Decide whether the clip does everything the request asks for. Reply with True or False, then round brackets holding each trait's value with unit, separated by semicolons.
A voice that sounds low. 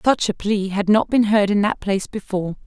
False (205 Hz)